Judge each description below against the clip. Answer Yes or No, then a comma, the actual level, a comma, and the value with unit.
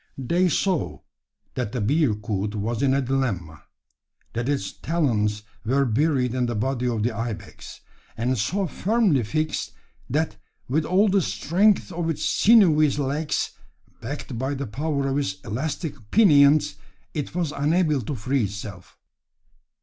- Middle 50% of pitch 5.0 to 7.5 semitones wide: Yes, wide, 5.6 semitones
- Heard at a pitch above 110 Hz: Yes, medium, 140 Hz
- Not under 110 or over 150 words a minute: Yes, average, 140 wpm